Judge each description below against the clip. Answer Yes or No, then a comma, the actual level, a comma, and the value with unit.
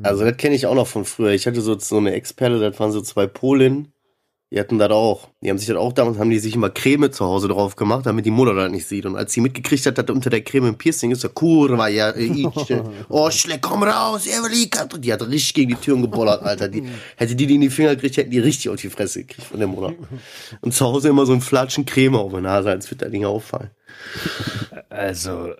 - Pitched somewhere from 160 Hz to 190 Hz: No, low, 120 Hz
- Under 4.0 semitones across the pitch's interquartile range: No, average, 4.5 semitones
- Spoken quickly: Yes, fast, 260 wpm